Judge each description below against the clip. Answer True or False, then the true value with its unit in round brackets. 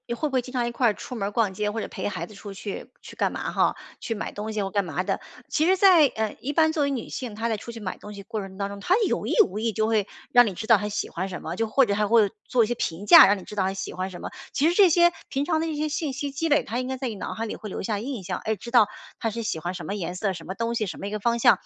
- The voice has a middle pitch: False (220 Hz)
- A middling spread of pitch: True (4.2 semitones)